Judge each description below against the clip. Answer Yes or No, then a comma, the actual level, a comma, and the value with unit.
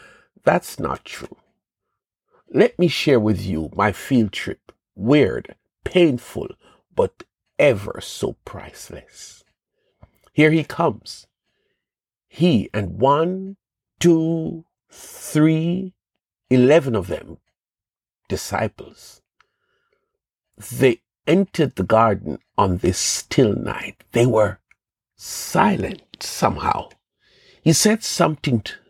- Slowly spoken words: Yes, slow, 95 wpm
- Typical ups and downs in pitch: No, wide, 8.3 semitones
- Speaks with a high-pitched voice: No, medium, 155 Hz